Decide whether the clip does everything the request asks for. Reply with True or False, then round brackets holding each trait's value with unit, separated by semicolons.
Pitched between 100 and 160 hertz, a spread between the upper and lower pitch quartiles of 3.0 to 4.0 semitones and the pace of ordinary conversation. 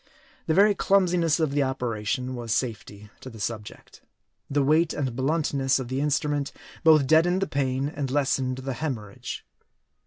True (135 Hz; 3.6 semitones; 155 wpm)